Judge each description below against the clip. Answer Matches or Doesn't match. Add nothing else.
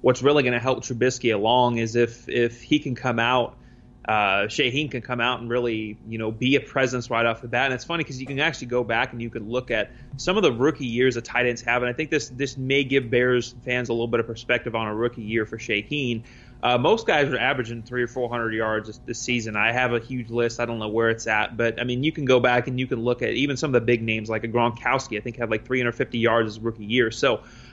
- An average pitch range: Doesn't match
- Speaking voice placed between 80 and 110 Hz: Doesn't match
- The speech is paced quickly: Matches